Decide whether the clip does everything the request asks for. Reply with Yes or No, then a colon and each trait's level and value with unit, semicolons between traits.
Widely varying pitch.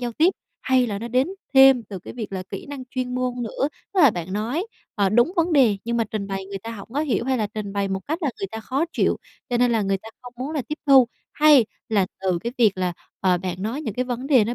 No: average, 4.8 semitones